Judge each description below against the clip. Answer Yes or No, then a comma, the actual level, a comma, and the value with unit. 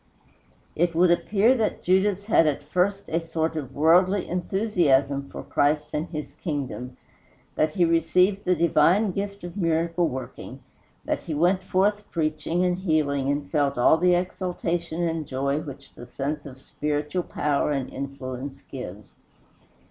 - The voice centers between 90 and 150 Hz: No, medium, 160 Hz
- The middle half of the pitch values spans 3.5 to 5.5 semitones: Yes, average, 4.1 semitones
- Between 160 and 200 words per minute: No, average, 150 wpm